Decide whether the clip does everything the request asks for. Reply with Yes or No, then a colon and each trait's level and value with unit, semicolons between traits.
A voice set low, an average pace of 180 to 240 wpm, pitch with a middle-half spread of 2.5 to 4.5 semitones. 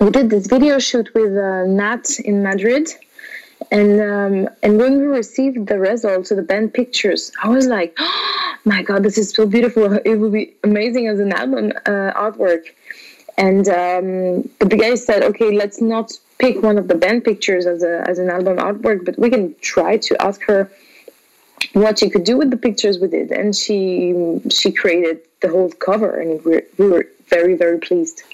No: high, 210 Hz; average, 195 wpm; average, 3.6 semitones